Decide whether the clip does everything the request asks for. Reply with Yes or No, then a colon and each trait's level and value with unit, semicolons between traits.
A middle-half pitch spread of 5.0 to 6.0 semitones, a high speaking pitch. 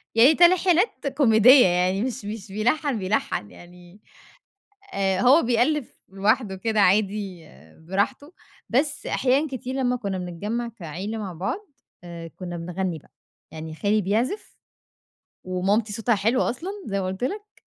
Yes: wide, 5.4 semitones; high, 215 Hz